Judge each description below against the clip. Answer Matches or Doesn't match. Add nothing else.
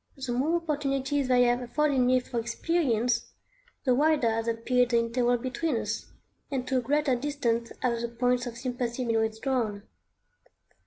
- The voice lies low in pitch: Doesn't match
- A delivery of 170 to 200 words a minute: Doesn't match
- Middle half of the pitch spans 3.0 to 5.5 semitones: Doesn't match